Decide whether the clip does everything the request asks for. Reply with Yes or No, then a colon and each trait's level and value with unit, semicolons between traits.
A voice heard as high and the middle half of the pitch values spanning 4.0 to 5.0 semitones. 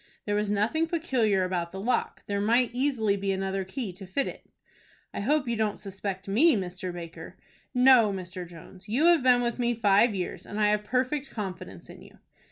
Yes: high, 210 Hz; average, 4.5 semitones